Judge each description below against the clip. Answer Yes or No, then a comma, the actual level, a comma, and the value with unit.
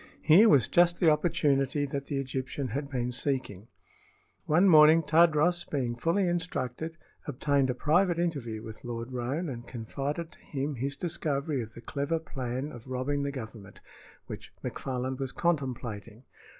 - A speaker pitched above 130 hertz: Yes, medium, 140 Hz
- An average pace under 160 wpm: Yes, average, 150 wpm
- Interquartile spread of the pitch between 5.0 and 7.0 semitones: No, average, 4.1 semitones